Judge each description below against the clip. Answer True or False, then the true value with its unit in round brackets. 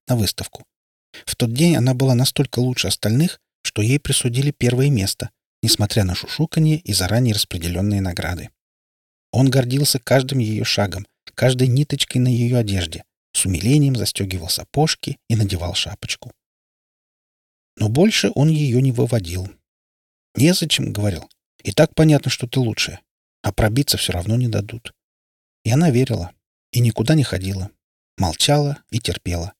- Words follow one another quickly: False (140 wpm)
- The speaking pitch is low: True (115 Hz)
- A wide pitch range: True (6.2 semitones)